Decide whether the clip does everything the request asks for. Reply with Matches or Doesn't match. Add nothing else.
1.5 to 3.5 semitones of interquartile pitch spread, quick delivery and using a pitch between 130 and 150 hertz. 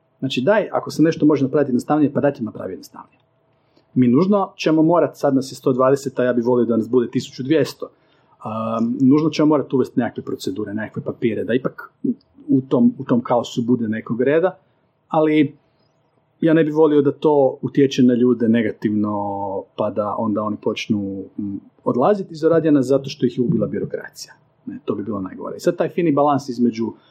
Doesn't match